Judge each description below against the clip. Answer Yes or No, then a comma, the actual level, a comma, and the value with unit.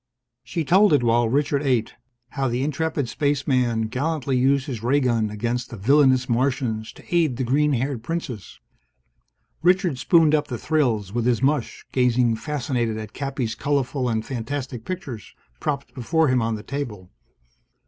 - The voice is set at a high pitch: No, low, 130 Hz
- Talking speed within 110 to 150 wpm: No, average, 160 wpm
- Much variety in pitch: No, average, 3.6 semitones